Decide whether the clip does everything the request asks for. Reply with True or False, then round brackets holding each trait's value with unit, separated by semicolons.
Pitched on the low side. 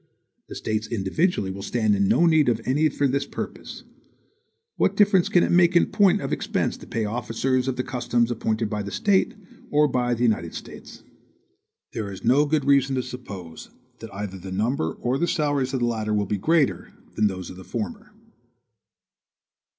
True (125 Hz)